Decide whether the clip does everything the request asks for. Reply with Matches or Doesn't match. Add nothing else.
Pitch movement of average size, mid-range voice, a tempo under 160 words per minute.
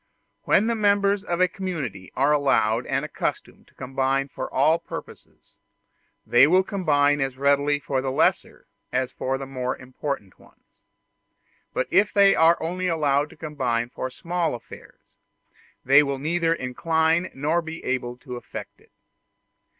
Matches